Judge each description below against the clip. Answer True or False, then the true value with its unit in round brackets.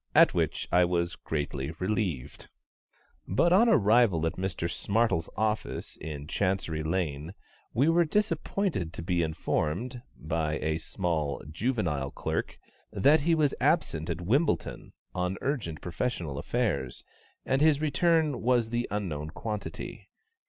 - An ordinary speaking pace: False (130 wpm)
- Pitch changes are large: True (7.6 semitones)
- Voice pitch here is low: True (95 Hz)